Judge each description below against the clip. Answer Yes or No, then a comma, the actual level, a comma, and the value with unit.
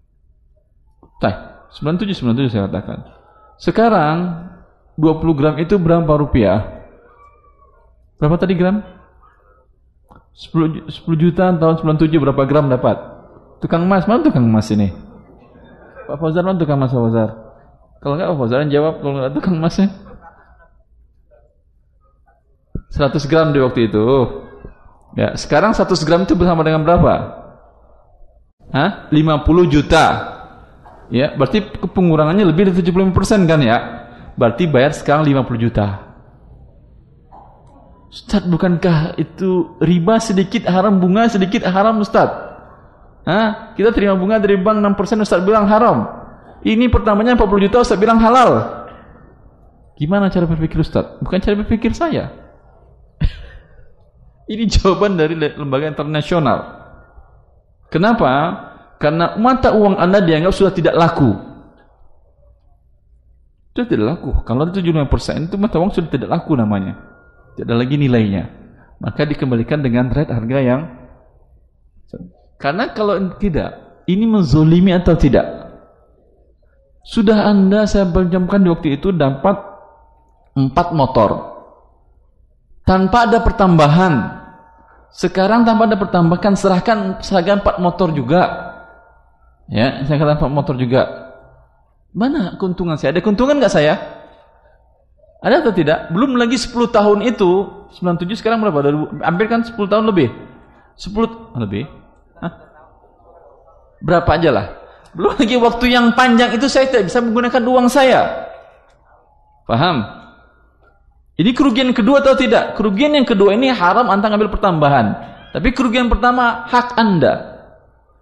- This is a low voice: No, medium, 175 Hz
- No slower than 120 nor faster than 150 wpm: Yes, average, 125 wpm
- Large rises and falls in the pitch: Yes, wide, 6.7 semitones